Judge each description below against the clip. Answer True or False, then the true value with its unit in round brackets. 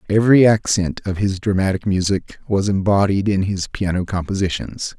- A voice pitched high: False (100 Hz)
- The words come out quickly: False (145 wpm)